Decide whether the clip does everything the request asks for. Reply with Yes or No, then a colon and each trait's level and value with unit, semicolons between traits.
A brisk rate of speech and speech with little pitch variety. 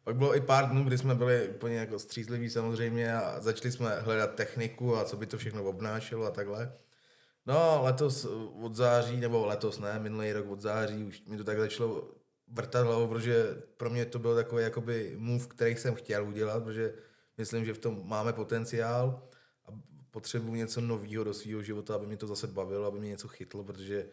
Yes: fast, 195 wpm; narrow, 1.9 semitones